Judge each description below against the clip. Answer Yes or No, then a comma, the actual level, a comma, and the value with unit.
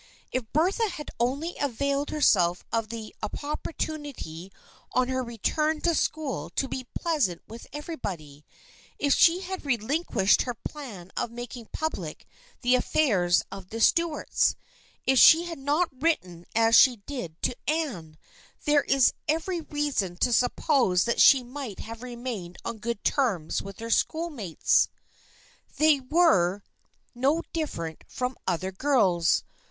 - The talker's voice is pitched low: No, very high, 250 Hz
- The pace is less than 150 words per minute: Yes, slow, 135 wpm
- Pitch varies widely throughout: Yes, wide, 7.0 semitones